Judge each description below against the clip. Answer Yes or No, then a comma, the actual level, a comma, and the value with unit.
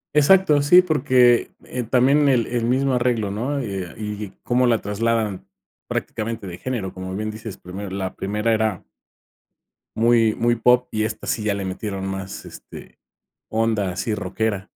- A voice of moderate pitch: No, low, 110 Hz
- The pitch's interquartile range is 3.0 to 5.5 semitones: Yes, average, 3.7 semitones